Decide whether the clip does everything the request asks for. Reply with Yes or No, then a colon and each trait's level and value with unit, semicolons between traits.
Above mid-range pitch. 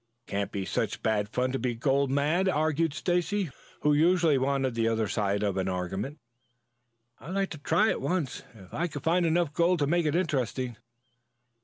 No: medium, 140 Hz